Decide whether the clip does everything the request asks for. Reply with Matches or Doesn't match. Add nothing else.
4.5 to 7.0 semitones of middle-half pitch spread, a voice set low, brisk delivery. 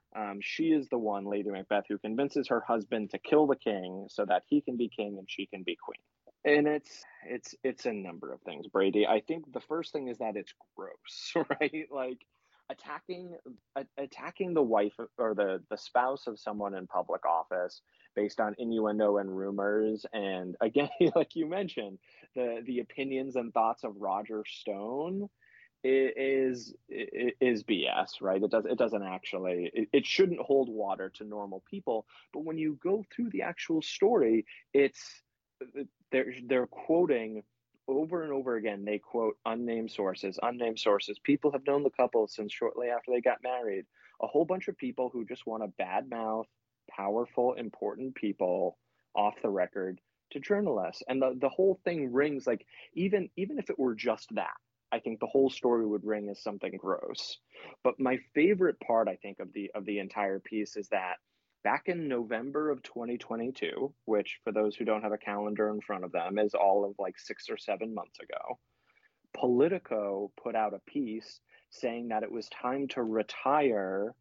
Doesn't match